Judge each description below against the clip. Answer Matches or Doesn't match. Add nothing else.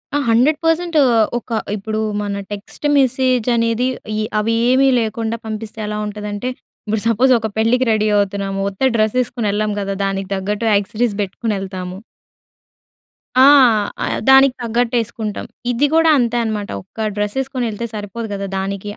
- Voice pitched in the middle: Doesn't match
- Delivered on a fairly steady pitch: Doesn't match